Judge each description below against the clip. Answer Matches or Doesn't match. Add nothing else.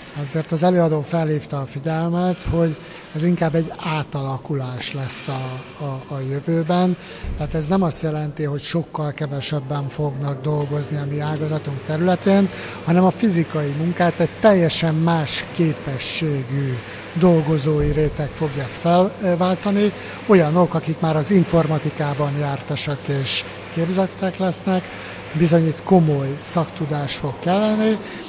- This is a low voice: Doesn't match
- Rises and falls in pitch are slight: Doesn't match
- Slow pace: Doesn't match